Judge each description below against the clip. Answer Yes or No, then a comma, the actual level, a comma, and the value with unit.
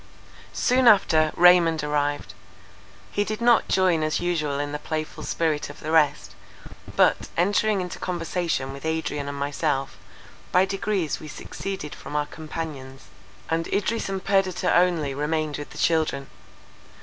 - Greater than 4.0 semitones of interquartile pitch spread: No, average, 3.7 semitones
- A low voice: No, medium, 160 Hz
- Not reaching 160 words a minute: Yes, average, 145 wpm